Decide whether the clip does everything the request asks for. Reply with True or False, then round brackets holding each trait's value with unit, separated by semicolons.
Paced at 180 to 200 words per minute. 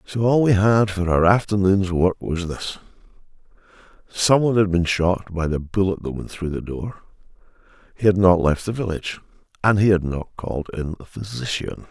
True (185 wpm)